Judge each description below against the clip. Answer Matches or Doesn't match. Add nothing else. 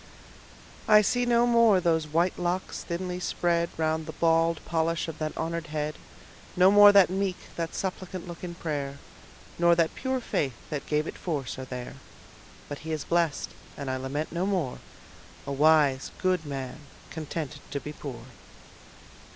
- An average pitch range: Matches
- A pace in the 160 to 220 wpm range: Matches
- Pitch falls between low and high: Matches